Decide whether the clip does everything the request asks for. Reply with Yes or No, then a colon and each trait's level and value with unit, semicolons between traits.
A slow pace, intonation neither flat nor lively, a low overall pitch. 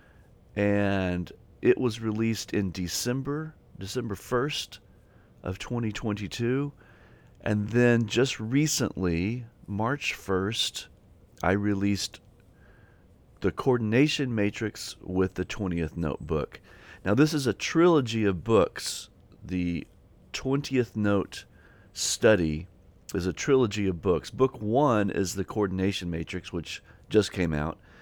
Yes: slow, 110 wpm; average, 4.4 semitones; low, 105 Hz